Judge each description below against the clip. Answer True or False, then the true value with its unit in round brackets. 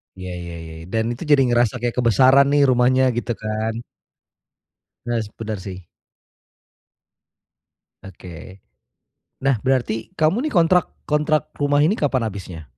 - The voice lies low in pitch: True (120 Hz)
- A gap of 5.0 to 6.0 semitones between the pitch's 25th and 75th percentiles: True (5.4 semitones)